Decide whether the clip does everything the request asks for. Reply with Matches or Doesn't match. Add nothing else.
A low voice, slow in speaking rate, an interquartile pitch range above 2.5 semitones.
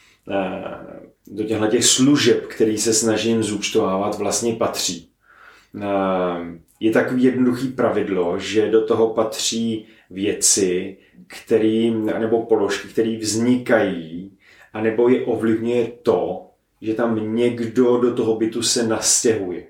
Doesn't match